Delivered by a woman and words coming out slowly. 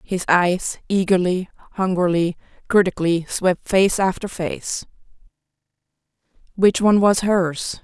Yes: female; slow, 100 wpm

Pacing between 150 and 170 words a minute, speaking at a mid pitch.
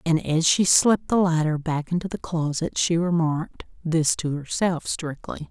Yes: average, 165 wpm; medium, 165 Hz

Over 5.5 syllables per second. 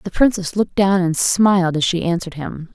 Yes: 5.8 syllables/s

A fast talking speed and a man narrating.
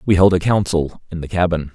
Yes: fast, 240 wpm; male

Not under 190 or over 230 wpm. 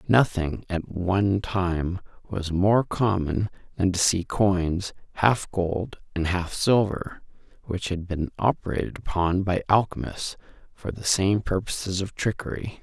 No: slow, 135 wpm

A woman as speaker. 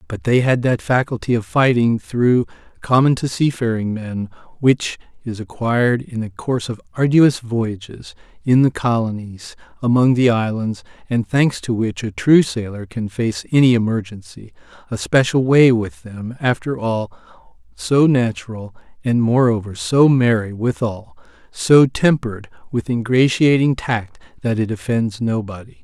No: male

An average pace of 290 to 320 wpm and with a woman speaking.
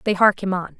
Yes: fast, 300 wpm; female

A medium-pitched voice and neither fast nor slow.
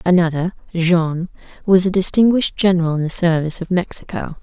Yes: medium, 175 Hz; average, 150 wpm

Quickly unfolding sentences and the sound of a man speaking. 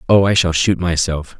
Yes: fast, 215 wpm; male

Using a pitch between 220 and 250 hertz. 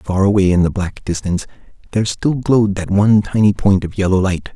No: low, 100 Hz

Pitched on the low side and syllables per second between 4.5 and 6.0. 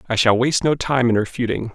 No: low, 120 Hz; 6.5 syllables/s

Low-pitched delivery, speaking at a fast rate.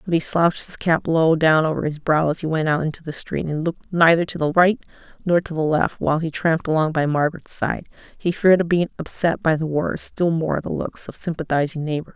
No: medium, 160 Hz; fast, 235 wpm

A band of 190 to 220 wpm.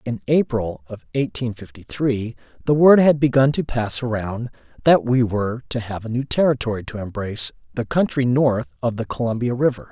No: average, 180 wpm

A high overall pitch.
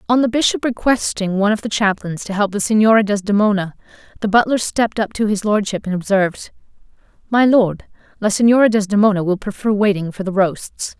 Yes: high, 205 Hz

